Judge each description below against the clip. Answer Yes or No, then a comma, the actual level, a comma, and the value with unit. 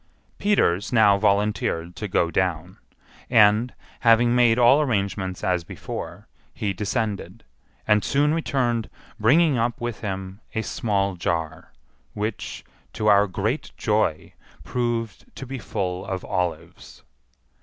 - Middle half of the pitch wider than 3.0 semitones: Yes, average, 4.1 semitones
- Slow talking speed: Yes, slow, 125 wpm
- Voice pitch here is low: Yes, low, 105 Hz